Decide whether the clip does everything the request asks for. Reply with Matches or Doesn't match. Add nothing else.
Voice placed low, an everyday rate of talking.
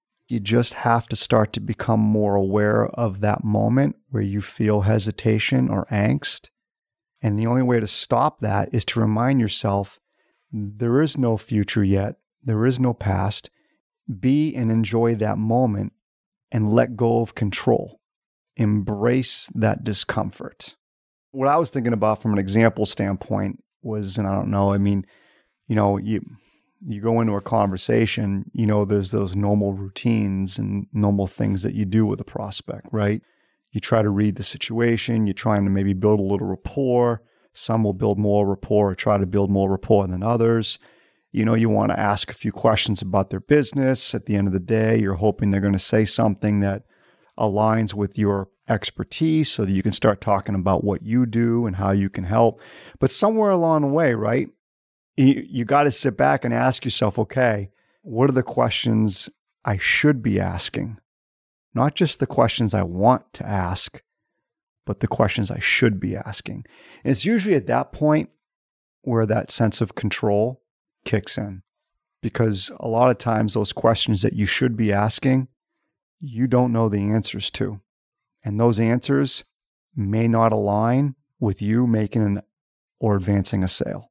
Matches